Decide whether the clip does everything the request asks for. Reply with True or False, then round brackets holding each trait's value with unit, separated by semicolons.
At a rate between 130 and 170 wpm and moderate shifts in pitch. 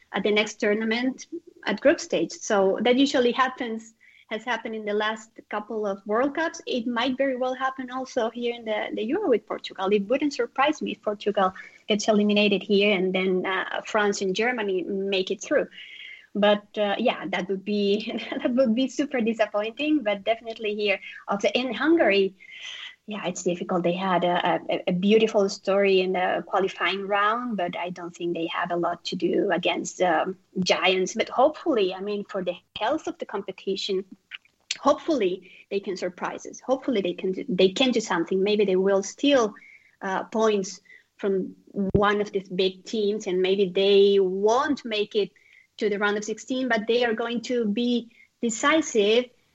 False (180 wpm; 4.0 semitones)